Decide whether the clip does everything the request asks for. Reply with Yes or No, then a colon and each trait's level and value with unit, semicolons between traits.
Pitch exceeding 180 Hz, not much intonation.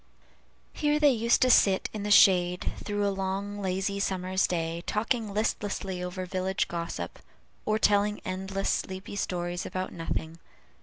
Yes: high, 190 Hz; narrow, 2.1 semitones